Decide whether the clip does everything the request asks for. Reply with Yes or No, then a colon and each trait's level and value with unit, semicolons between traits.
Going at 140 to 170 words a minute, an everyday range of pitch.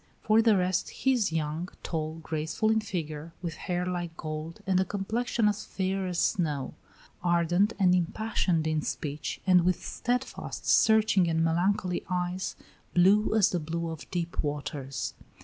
Yes: average, 155 wpm; average, 3.3 semitones